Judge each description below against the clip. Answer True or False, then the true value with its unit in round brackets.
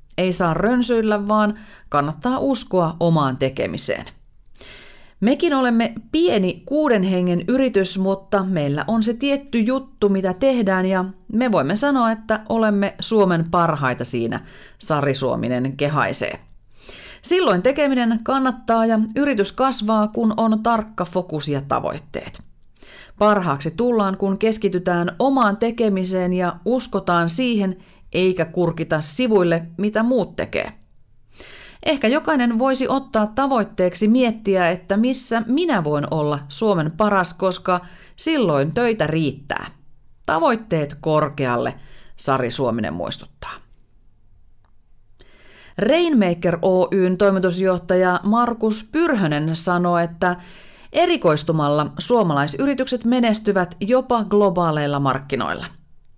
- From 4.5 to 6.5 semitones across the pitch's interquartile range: True (5.3 semitones)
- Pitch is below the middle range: False (200 Hz)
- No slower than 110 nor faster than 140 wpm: False (100 wpm)